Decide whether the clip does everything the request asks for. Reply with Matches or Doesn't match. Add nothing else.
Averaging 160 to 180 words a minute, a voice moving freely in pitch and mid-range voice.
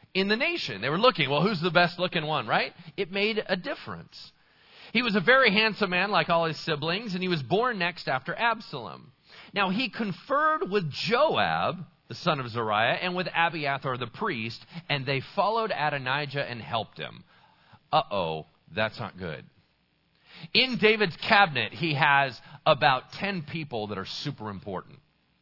Matches